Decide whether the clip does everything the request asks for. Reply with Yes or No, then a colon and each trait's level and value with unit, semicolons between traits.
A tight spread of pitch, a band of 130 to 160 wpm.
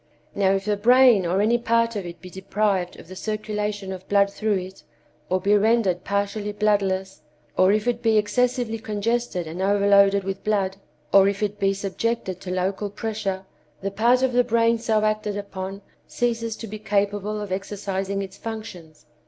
No: narrow, 2.2 semitones; average, 175 wpm